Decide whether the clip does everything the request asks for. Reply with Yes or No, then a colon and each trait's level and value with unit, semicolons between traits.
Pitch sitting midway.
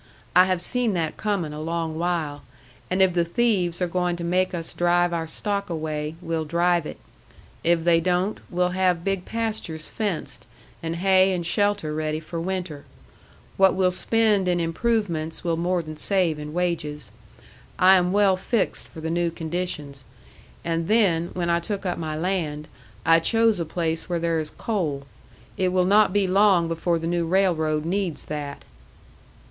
Yes: medium, 175 Hz